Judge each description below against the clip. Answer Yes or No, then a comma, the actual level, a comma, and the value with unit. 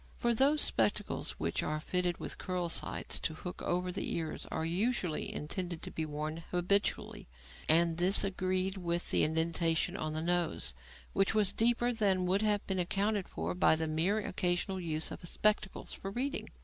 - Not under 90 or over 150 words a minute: No, average, 175 wpm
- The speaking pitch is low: No, medium, 180 Hz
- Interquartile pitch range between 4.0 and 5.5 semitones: No, average, 3.5 semitones